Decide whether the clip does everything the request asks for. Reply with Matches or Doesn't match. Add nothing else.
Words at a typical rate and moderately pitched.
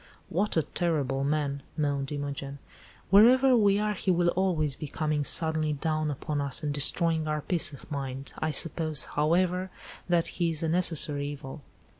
Matches